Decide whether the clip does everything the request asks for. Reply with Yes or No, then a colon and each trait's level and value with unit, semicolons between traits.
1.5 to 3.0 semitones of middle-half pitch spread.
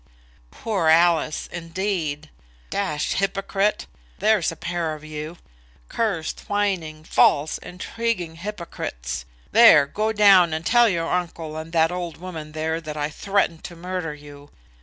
No: average, 3.9 semitones